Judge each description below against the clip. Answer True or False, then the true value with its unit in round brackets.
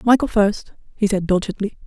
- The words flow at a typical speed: True (160 wpm)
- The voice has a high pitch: True (205 Hz)